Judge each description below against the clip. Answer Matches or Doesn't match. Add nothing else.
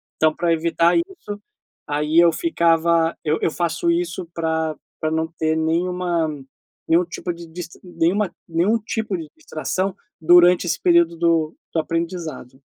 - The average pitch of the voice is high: Doesn't match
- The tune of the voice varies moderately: Doesn't match